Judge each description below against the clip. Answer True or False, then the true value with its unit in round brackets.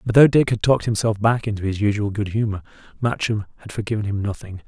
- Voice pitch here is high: False (105 Hz)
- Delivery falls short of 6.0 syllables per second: False (6.5 syllables/s)